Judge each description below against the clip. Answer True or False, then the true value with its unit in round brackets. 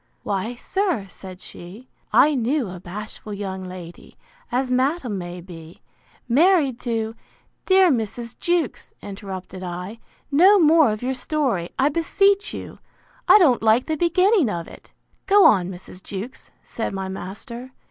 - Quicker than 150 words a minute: False (140 wpm)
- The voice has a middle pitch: False (230 Hz)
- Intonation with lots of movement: True (8.2 semitones)